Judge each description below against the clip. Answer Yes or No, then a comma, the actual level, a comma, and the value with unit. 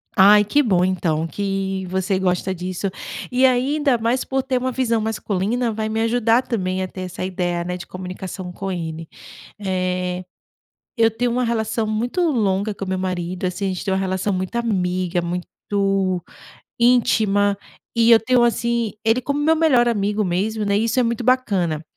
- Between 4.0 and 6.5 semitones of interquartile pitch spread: Yes, average, 4.3 semitones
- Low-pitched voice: No, high, 205 Hz